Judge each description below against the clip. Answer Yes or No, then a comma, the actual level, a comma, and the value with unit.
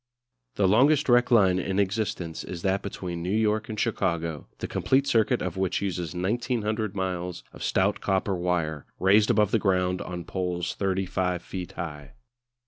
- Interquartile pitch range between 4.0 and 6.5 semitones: No, average, 3.1 semitones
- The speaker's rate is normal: Yes, average, 160 wpm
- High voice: No, very low, 95 Hz